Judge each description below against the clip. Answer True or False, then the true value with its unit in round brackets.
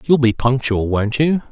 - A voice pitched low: True (125 Hz)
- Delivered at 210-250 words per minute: False (200 wpm)